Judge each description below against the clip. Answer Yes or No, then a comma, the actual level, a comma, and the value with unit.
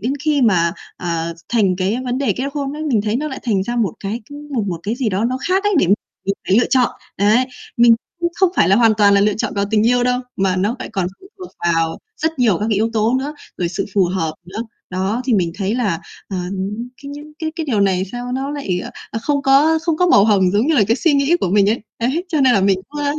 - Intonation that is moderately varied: No, wide, 5.9 semitones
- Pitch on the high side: Yes, high, 230 Hz